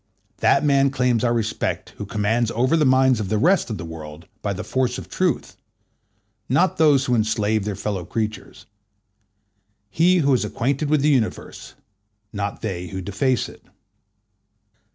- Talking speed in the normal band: Yes, average, 160 wpm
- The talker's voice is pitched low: Yes, low, 115 Hz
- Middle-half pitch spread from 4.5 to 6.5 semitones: Yes, average, 5.0 semitones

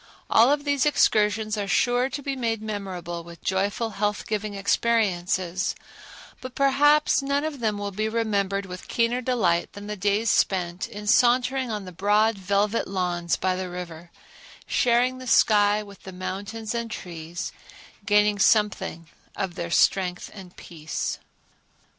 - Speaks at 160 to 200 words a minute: No, average, 150 wpm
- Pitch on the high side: Yes, high, 205 Hz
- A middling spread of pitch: Yes, average, 3.8 semitones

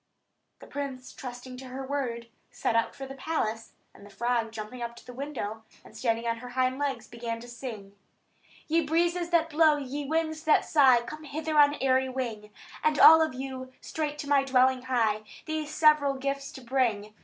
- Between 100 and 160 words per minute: No, average, 190 wpm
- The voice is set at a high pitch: Yes, very high, 260 Hz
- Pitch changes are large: No, average, 3.7 semitones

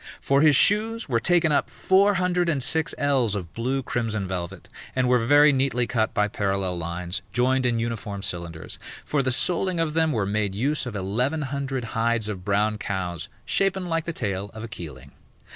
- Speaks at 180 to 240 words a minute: Yes, average, 190 wpm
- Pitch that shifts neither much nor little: No, wide, 6.8 semitones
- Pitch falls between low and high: No, low, 120 Hz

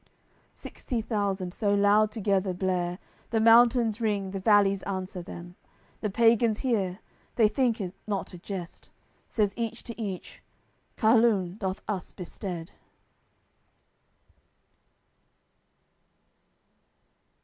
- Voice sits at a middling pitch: No, high, 205 Hz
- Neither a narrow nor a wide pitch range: Yes, average, 3.1 semitones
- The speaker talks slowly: Yes, slow, 105 wpm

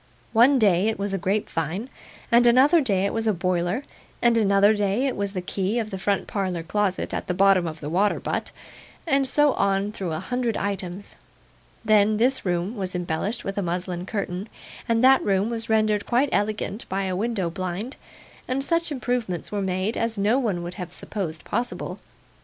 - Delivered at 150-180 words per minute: No, average, 190 wpm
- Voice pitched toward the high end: Yes, high, 200 Hz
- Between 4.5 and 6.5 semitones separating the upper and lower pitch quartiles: No, average, 3.7 semitones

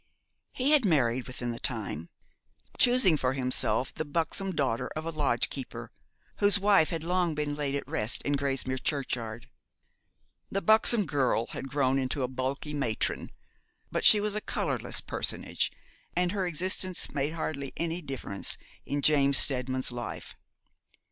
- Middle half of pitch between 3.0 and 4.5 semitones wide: No, average, 5.1 semitones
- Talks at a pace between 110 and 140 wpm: No, average, 150 wpm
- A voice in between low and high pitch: Yes, medium, 145 Hz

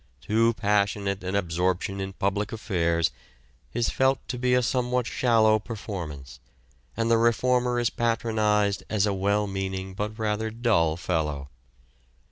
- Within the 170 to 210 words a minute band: No, slow, 135 wpm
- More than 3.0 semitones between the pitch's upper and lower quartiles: Yes, average, 3.4 semitones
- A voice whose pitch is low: Yes, low, 105 Hz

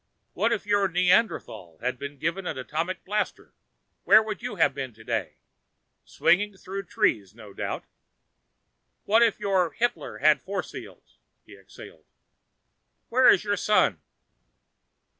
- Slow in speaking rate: Yes, slow, 130 wpm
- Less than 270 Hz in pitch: Yes, medium, 185 Hz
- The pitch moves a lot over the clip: Yes, wide, 6.7 semitones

